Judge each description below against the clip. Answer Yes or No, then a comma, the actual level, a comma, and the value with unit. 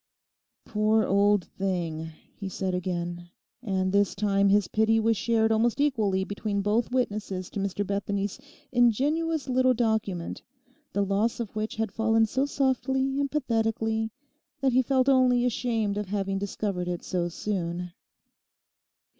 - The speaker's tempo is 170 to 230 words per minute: No, average, 140 wpm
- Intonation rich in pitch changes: No, average, 3.7 semitones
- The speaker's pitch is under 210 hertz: No, high, 215 Hz